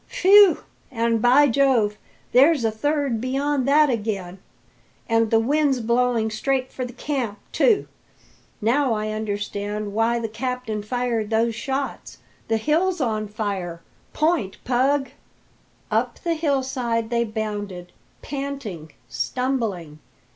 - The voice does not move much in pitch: No, average, 4.1 semitones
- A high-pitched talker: Yes, high, 235 Hz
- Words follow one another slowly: Yes, slow, 120 wpm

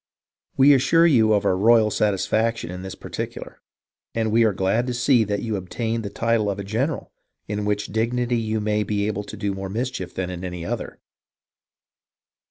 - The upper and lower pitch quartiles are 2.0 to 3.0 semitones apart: Yes, average, 2.7 semitones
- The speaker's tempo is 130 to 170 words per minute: No, average, 190 wpm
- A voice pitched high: No, low, 110 Hz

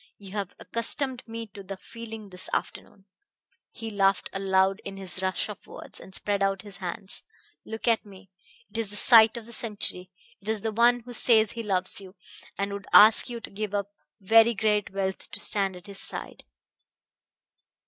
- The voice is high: Yes, high, 205 Hz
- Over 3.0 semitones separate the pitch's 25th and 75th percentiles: No, narrow, 2.5 semitones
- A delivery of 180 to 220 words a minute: Yes, average, 190 wpm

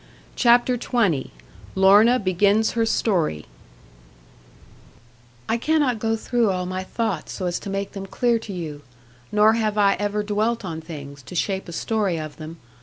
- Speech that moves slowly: No, average, 160 wpm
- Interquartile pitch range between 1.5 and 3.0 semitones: No, average, 3.9 semitones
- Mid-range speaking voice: No, high, 205 Hz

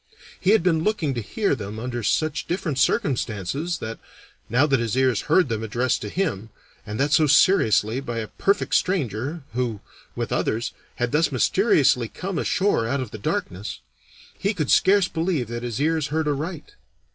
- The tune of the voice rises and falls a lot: Yes, wide, 6.3 semitones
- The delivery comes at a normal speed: Yes, average, 175 wpm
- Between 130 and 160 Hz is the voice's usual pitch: Yes, low, 135 Hz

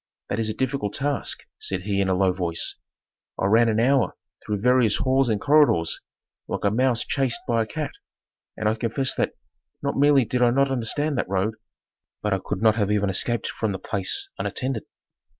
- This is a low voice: Yes, low, 115 Hz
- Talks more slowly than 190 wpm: No, average, 195 wpm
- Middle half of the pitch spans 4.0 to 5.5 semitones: Yes, average, 4.6 semitones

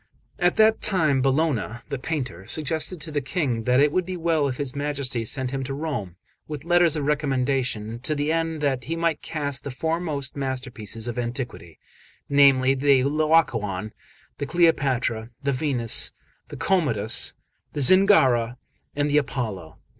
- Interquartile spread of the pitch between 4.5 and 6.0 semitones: No, average, 4.0 semitones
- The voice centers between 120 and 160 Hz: Yes, medium, 140 Hz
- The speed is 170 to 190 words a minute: No, average, 160 wpm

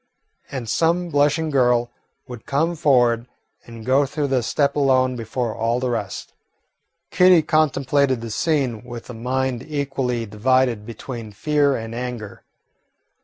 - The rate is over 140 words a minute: No, slow, 135 wpm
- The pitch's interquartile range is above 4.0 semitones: No, average, 3.4 semitones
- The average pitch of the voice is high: No, low, 130 Hz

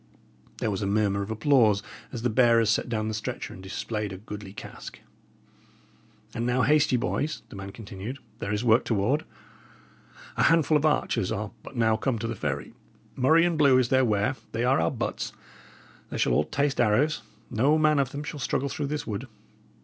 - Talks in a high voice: No, low, 120 Hz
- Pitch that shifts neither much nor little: Yes, average, 4.8 semitones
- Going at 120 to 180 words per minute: No, average, 195 wpm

